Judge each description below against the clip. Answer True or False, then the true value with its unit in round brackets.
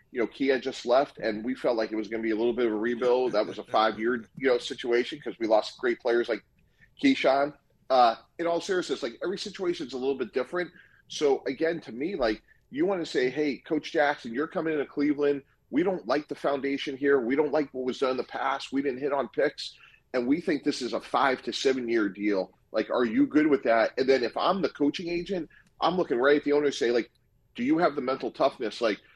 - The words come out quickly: True (250 wpm)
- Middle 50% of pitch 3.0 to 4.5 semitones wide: False (5.6 semitones)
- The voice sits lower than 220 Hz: True (140 Hz)